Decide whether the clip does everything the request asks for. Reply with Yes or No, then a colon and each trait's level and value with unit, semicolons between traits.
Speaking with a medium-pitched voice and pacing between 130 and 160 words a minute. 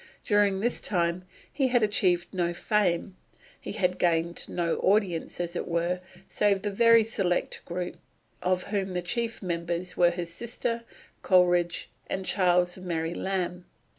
Yes: medium, 180 Hz; average, 150 wpm